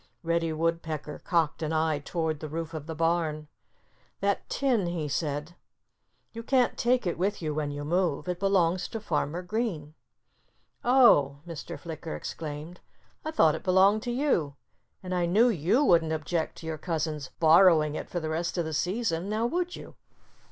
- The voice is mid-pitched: Yes, medium, 165 Hz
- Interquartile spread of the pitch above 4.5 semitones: No, average, 3.7 semitones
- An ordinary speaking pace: Yes, average, 165 wpm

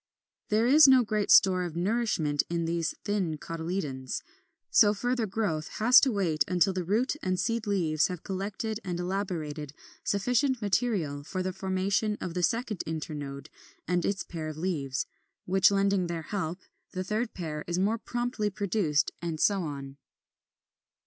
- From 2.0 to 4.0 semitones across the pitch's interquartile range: No, average, 4.6 semitones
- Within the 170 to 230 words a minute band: No, average, 155 wpm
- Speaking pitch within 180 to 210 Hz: Yes, medium, 185 Hz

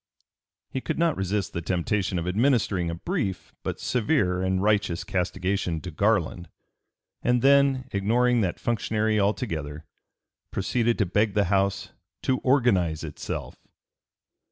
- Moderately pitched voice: No, low, 100 Hz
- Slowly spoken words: Yes, slow, 130 wpm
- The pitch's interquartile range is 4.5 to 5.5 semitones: Yes, average, 5.0 semitones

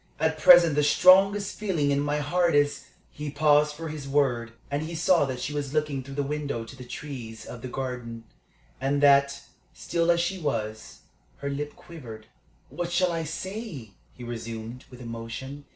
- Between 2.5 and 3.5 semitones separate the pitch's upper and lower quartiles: No, average, 4.3 semitones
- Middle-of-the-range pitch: Yes, medium, 145 Hz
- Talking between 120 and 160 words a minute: No, average, 185 wpm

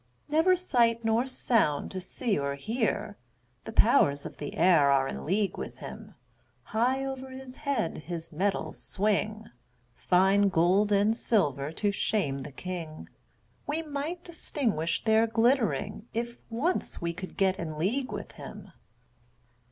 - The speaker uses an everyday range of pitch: No, wide, 6.4 semitones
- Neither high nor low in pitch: No, high, 210 Hz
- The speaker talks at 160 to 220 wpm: No, average, 145 wpm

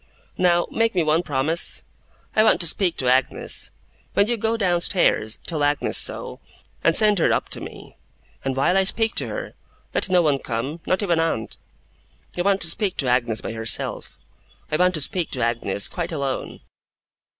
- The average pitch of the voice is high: No, medium, 165 Hz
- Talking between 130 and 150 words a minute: No, average, 185 wpm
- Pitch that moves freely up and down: Yes, wide, 6.0 semitones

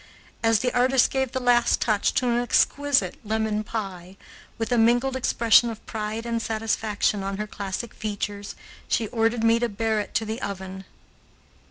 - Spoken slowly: No, average, 170 wpm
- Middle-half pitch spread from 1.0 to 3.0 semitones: Yes, narrow, 2.4 semitones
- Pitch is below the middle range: No, high, 225 Hz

